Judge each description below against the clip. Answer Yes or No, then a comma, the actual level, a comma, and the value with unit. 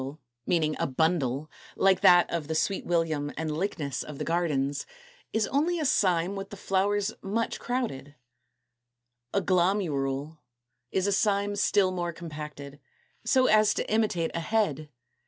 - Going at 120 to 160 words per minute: Yes, average, 155 wpm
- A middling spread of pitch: Yes, average, 5.0 semitones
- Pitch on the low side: No, medium, 175 Hz